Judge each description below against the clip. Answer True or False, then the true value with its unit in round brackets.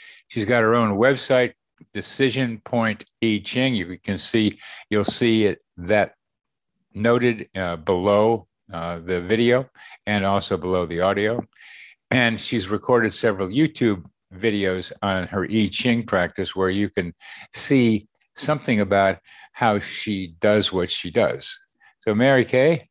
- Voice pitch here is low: True (105 Hz)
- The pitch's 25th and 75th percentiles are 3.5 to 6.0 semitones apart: True (4.1 semitones)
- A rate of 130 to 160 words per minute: True (140 wpm)